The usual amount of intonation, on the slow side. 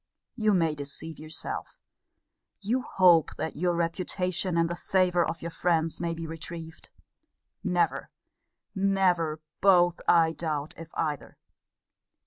No: narrow, 2.1 semitones; slow, 120 wpm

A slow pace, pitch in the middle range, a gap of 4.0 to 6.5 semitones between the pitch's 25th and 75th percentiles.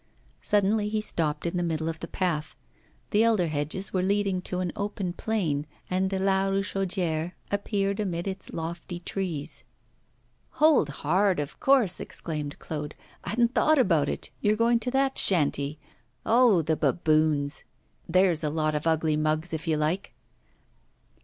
No: average, 155 wpm; medium, 180 Hz; average, 4.4 semitones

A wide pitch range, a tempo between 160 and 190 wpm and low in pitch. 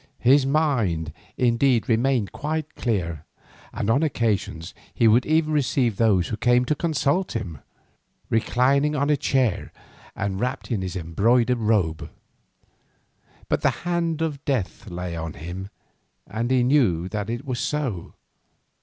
No: wide, 6.4 semitones; average, 140 wpm; low, 120 Hz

